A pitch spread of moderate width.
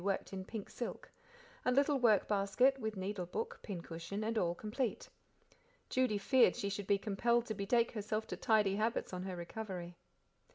Yes: average, 3.2 semitones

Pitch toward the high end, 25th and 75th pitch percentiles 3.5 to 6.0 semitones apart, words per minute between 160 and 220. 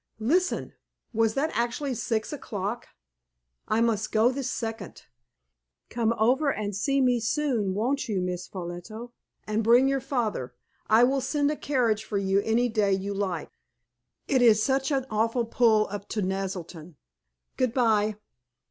No: high, 225 Hz; average, 4.0 semitones; average, 150 wpm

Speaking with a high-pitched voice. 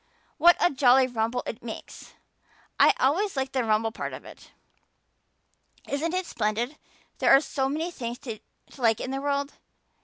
Yes: very high, 265 Hz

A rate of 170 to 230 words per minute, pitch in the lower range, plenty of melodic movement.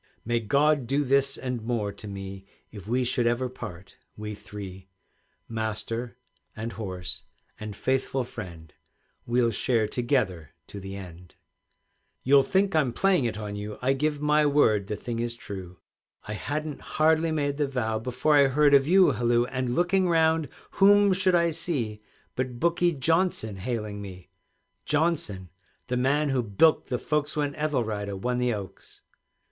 No: average, 160 wpm; low, 125 Hz; wide, 5.8 semitones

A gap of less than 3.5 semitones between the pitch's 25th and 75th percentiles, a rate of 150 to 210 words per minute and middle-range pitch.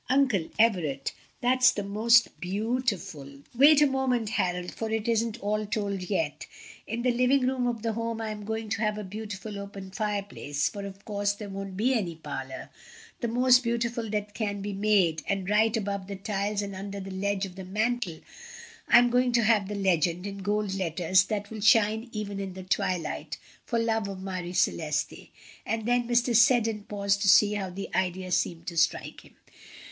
No: average, 3.1 semitones; average, 190 wpm; high, 205 Hz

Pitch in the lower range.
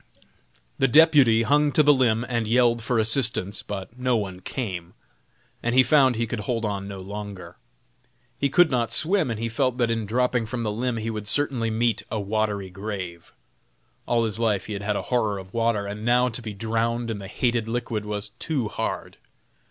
Yes: low, 115 Hz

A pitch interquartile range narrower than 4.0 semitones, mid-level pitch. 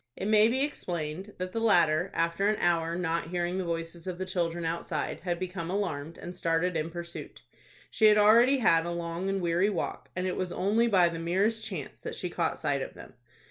Yes: average, 3.0 semitones; medium, 175 Hz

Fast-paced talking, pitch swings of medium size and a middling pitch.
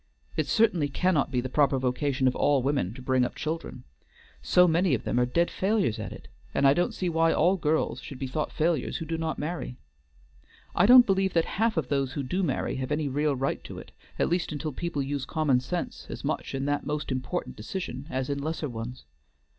Yes: fast, 220 wpm; average, 4.2 semitones; medium, 145 Hz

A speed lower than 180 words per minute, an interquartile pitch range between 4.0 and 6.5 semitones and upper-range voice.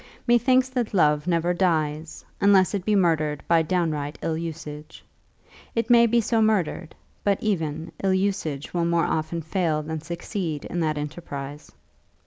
No: average, 150 wpm; average, 4.3 semitones; medium, 170 Hz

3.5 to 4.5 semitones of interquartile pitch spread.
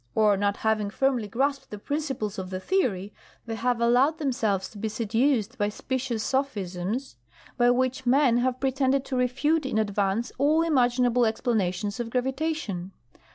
Yes: average, 4.2 semitones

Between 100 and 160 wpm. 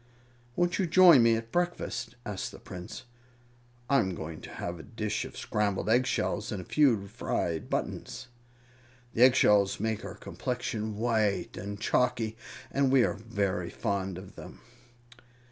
Yes: average, 150 wpm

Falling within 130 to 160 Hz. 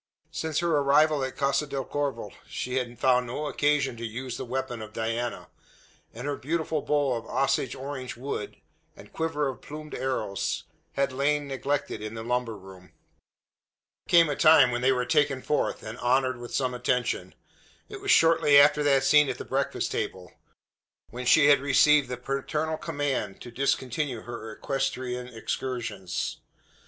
Yes: low, 135 Hz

